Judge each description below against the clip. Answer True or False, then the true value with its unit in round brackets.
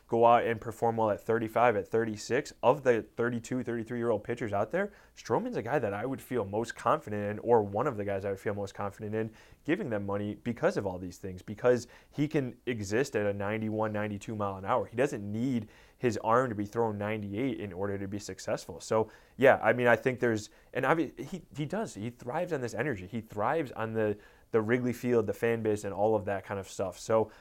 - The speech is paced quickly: True (235 wpm)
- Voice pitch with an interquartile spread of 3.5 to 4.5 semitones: False (2.8 semitones)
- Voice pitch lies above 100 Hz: True (110 Hz)